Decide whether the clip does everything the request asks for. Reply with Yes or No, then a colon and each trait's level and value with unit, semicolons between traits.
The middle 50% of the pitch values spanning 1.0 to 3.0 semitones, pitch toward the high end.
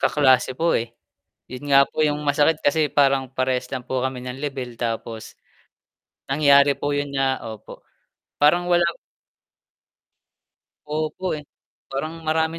No: average, 2.7 semitones; medium, 140 Hz